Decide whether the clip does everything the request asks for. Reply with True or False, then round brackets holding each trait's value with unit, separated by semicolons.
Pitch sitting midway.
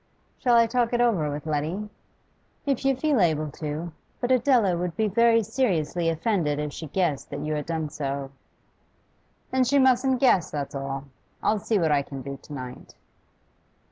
True (175 Hz)